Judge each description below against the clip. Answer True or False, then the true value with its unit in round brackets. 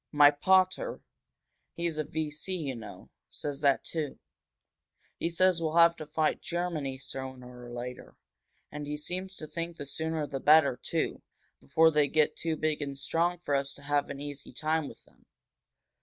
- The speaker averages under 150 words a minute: False (175 wpm)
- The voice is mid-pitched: True (150 Hz)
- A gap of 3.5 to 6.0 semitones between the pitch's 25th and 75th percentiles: False (2.8 semitones)